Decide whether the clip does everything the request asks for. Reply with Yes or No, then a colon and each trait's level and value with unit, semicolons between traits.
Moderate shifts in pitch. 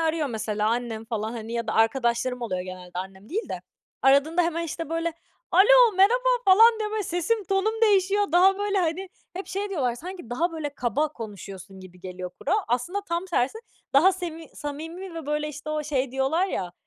No: wide, 8.3 semitones